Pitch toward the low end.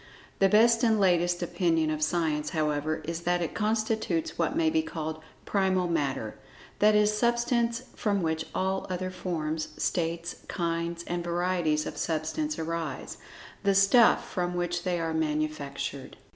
No: medium, 175 Hz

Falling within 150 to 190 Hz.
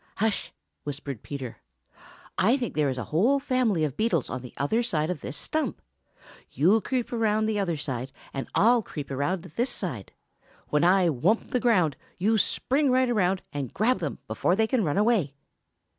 Yes: medium, 185 Hz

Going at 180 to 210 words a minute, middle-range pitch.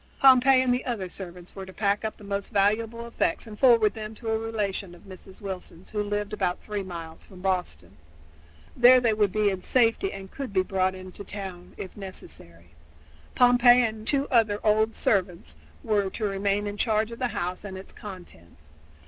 No: average, 195 wpm; high, 205 Hz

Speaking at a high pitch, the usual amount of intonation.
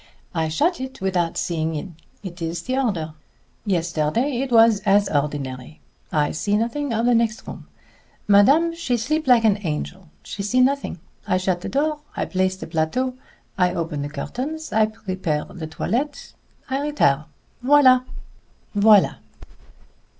No: high, 205 Hz; wide, 7.6 semitones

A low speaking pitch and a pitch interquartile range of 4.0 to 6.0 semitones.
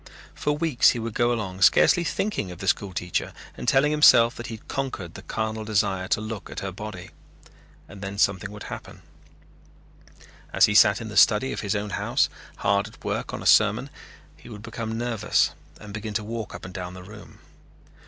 No: low, 105 Hz; average, 2.7 semitones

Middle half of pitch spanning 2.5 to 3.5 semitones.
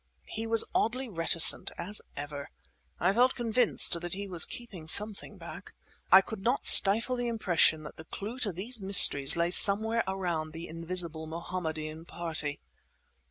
No: average, 5.2 semitones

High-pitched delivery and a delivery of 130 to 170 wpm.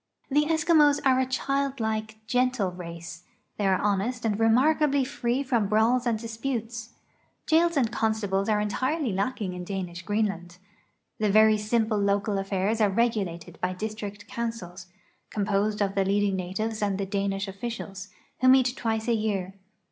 Yes: high, 215 Hz; average, 155 wpm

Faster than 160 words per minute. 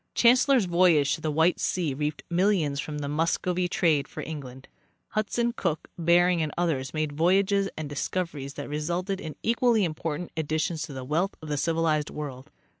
Yes: average, 180 wpm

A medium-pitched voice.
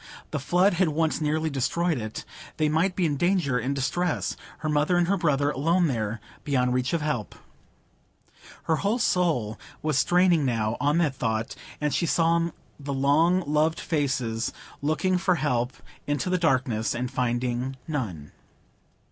Yes: medium, 150 Hz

